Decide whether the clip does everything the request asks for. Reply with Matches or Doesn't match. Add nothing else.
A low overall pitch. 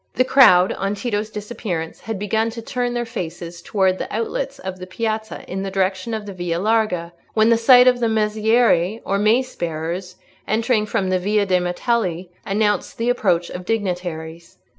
Doesn't match